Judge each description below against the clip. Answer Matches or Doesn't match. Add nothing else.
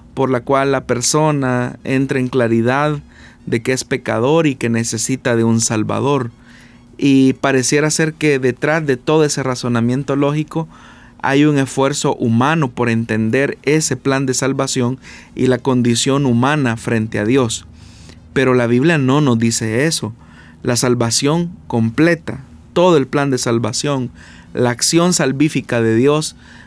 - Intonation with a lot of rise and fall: Doesn't match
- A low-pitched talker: Matches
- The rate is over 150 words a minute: Doesn't match